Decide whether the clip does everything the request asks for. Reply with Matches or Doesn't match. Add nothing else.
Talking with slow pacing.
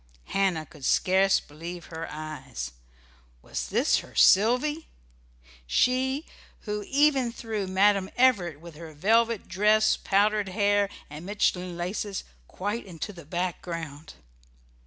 Matches